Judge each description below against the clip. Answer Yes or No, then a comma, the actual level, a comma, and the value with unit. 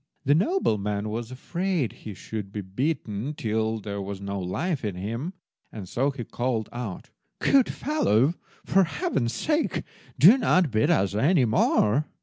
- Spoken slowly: No, average, 150 wpm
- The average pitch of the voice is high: No, low, 115 Hz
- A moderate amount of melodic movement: No, wide, 7.5 semitones